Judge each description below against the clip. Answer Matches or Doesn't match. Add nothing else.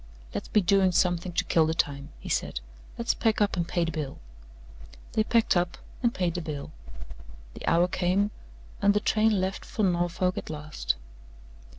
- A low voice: Doesn't match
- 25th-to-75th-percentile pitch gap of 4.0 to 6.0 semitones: Doesn't match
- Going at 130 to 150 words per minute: Doesn't match